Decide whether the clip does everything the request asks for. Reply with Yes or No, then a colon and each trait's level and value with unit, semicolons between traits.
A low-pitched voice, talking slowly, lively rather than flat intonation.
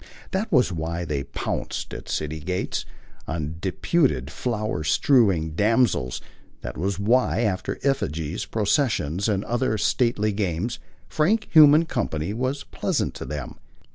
Yes: low, 100 Hz; slow, 130 wpm; wide, 7.8 semitones